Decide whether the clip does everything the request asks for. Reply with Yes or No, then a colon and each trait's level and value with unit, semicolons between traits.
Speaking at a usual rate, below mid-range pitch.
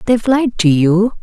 No: average, 195 wpm; high, 210 Hz